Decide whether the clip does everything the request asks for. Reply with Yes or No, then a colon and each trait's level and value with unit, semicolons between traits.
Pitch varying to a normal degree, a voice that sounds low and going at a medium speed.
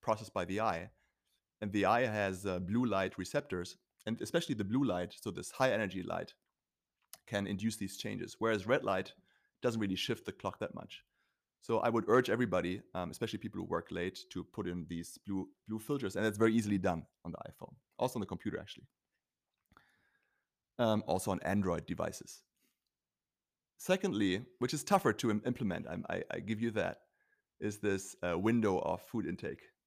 Yes: average, 3.6 semitones; low, 105 Hz; average, 185 wpm